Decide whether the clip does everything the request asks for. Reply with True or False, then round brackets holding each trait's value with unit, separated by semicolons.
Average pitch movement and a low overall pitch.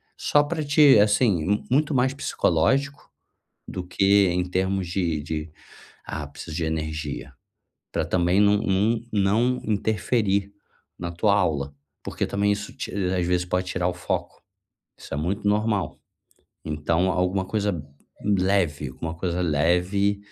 True (3.0 semitones; 95 Hz)